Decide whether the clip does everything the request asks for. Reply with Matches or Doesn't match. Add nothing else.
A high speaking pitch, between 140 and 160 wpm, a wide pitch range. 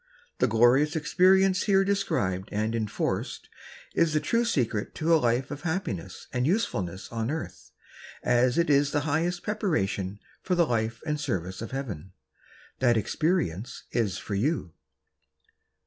Doesn't match